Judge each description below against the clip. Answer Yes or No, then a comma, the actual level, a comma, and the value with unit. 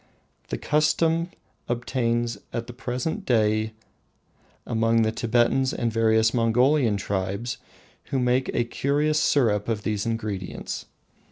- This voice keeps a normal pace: No, slow, 115 wpm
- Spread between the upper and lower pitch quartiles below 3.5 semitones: Yes, average, 2.8 semitones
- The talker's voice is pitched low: Yes, low, 115 Hz